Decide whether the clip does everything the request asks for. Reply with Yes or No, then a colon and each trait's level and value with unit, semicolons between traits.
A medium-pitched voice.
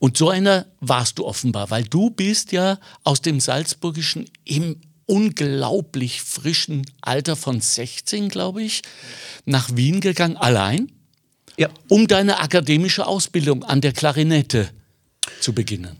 Yes: medium, 150 Hz